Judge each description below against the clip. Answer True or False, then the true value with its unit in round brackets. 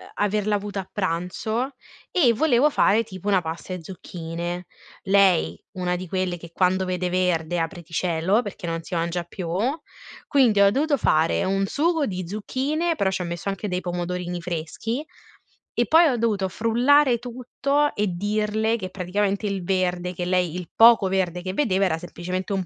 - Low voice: False (190 Hz)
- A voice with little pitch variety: False (3.8 semitones)